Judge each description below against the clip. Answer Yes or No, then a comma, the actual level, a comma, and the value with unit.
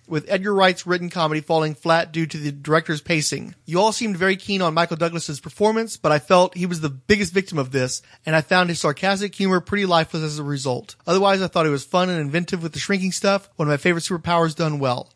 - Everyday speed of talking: No, fast, 240 wpm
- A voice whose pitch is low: No, medium, 170 Hz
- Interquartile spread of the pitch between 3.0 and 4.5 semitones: Yes, average, 3.4 semitones